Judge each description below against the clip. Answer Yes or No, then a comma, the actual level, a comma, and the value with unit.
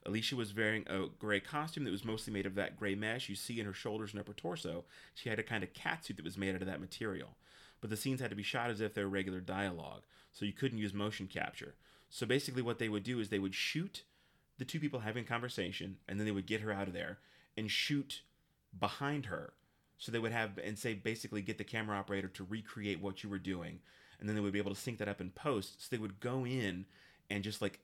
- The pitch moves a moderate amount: Yes, average, 3.1 semitones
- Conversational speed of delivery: No, fast, 255 wpm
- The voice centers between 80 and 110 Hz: Yes, low, 105 Hz